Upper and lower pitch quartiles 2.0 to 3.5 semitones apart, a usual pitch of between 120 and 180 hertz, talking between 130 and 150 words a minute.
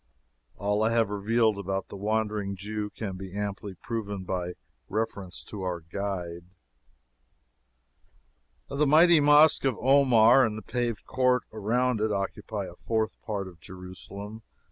No: average, 3.0 semitones; low, 105 Hz; average, 140 wpm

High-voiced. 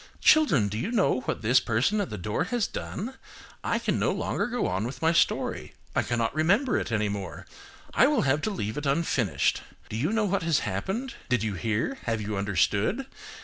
No: low, 135 Hz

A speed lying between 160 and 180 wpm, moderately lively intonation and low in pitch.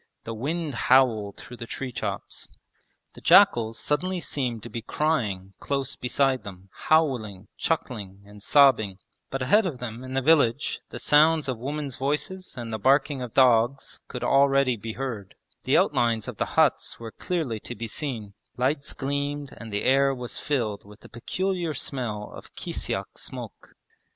Yes: average, 165 wpm; average, 4.1 semitones; low, 130 Hz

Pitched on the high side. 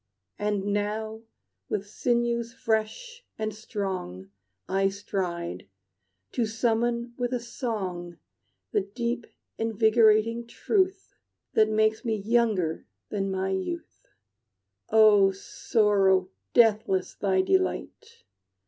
Yes: high, 215 Hz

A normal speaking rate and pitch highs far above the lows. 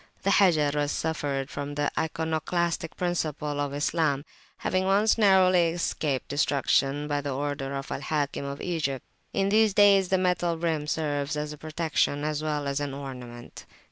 No: average, 160 wpm; average, 3.2 semitones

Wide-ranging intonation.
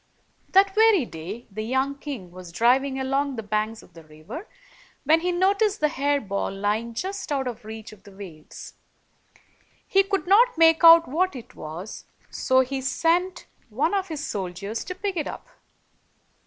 Yes: wide, 8.6 semitones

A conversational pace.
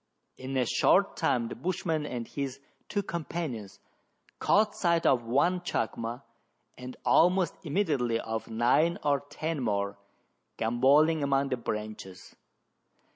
No: slow, 125 wpm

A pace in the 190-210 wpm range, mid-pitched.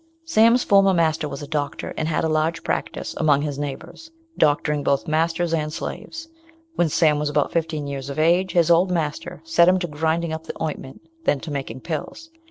Yes: average, 195 wpm; medium, 160 Hz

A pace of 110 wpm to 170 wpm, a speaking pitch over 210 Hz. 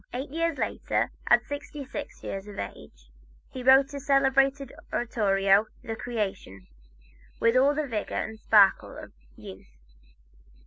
Yes: slow, 135 wpm; high, 245 Hz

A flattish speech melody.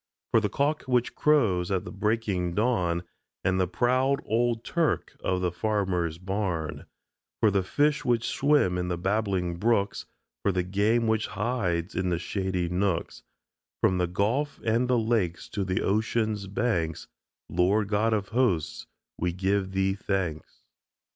No: average, 4.1 semitones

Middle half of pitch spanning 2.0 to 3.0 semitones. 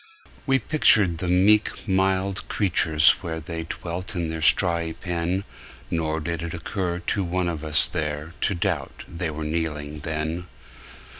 Yes: average, 2.7 semitones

